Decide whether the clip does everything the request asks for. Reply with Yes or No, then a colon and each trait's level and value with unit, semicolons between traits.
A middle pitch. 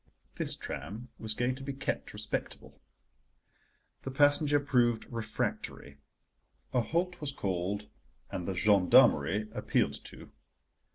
No: low, 115 Hz